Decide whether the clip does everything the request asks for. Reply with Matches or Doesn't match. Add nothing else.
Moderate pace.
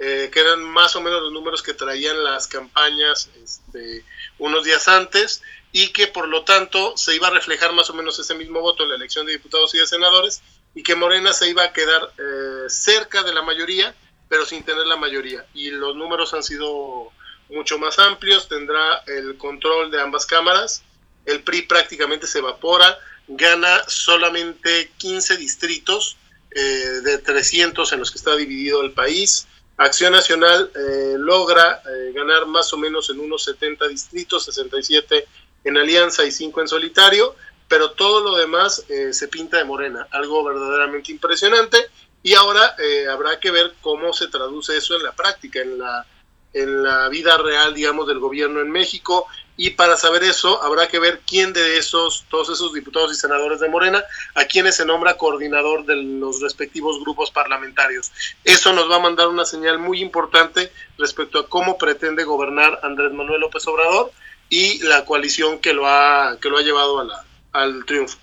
Matches